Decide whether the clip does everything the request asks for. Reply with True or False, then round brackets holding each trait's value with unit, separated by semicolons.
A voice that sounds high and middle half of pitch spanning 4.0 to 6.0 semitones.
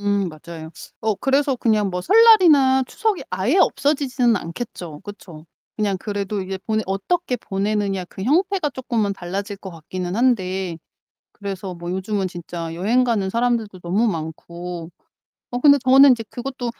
True (205 Hz; 5.5 semitones)